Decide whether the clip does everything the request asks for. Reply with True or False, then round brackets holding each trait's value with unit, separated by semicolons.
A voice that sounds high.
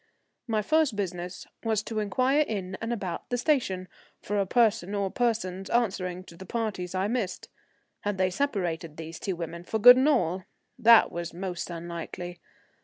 True (195 Hz)